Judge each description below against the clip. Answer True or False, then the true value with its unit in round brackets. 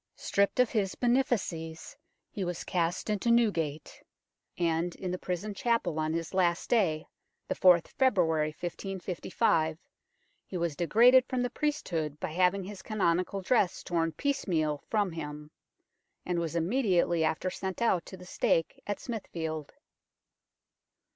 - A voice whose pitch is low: False (180 Hz)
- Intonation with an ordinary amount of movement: True (4.2 semitones)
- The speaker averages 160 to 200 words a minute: False (140 wpm)